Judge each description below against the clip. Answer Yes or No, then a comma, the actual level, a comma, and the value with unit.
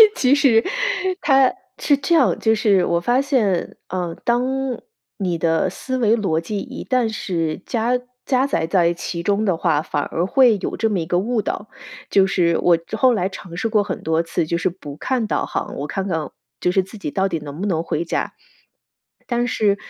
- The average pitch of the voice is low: No, high, 195 Hz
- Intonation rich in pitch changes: Yes, wide, 5.7 semitones